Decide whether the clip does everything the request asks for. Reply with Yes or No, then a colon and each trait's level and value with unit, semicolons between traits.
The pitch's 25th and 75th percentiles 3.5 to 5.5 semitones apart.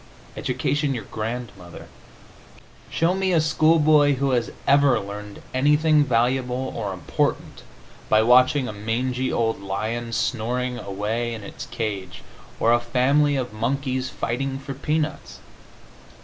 Yes: average, 3.8 semitones